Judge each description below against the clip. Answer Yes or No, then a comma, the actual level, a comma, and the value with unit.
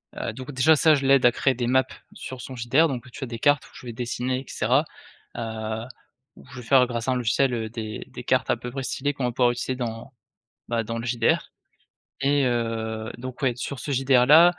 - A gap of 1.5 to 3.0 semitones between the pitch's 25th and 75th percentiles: Yes, narrow, 2.4 semitones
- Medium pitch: No, low, 125 Hz